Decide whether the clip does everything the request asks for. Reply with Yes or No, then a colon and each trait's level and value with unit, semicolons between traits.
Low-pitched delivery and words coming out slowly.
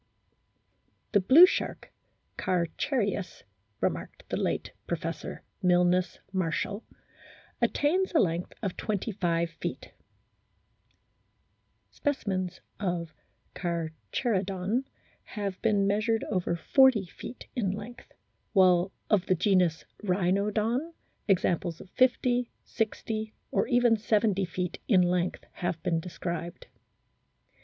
No: high, 190 Hz; slow, 100 wpm